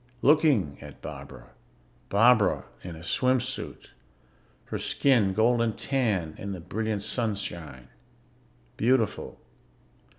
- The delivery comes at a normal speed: No, slow, 100 wpm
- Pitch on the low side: Yes, low, 110 Hz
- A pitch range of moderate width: No, wide, 5.9 semitones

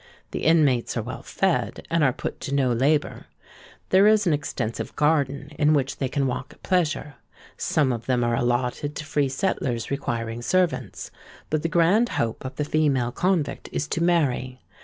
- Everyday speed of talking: Yes, average, 180 wpm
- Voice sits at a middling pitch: Yes, medium, 145 Hz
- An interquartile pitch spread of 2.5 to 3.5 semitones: No, average, 4.4 semitones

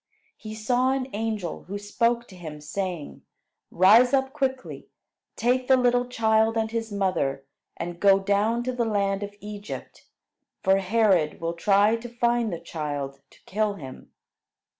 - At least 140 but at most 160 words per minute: Yes, average, 155 wpm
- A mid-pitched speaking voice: No, high, 210 Hz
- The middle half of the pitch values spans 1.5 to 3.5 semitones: No, average, 4.3 semitones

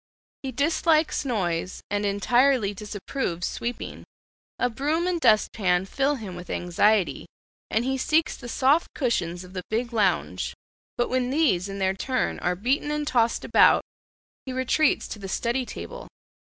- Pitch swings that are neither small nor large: No, wide, 5.9 semitones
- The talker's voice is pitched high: Yes, high, 235 Hz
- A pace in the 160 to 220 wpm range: No, average, 150 wpm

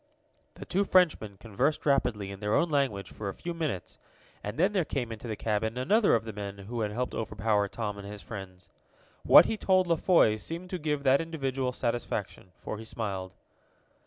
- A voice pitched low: Yes, low, 115 Hz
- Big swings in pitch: Yes, wide, 6.8 semitones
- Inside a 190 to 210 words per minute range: Yes, average, 195 wpm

